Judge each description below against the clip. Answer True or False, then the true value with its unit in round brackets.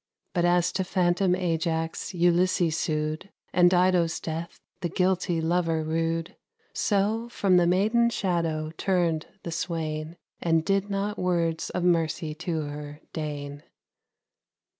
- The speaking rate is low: True (125 wpm)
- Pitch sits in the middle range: True (170 Hz)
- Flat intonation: True (2.2 semitones)